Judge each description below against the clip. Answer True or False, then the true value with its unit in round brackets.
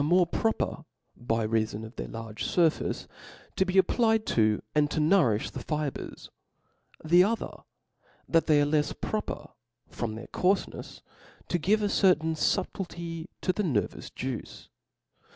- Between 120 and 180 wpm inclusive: True (150 wpm)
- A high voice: False (160 Hz)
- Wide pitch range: True (7.4 semitones)